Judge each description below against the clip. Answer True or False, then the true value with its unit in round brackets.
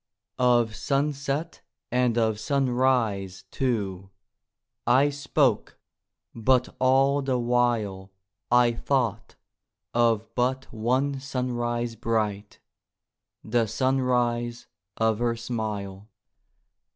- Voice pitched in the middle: False (120 Hz)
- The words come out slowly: True (85 wpm)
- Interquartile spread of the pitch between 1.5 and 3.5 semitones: True (2.8 semitones)